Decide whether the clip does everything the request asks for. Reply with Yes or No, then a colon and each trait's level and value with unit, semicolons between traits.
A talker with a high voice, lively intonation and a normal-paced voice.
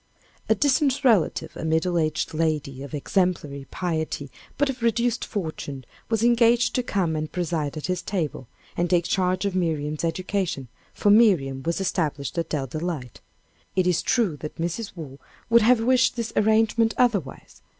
No: medium, 175 Hz; wide, 6.4 semitones; average, 160 wpm